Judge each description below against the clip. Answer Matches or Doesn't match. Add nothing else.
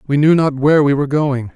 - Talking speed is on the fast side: Matches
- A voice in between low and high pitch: Matches